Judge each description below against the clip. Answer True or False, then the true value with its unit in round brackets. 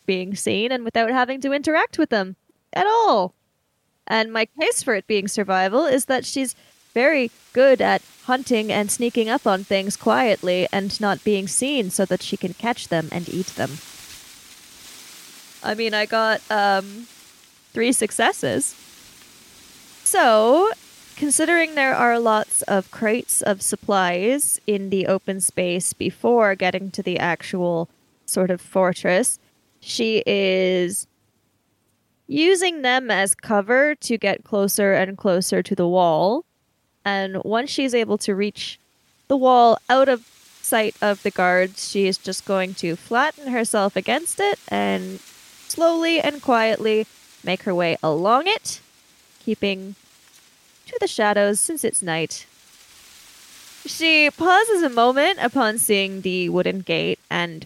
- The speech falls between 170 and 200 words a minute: False (140 wpm)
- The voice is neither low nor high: False (210 Hz)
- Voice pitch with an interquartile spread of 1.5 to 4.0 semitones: False (5.0 semitones)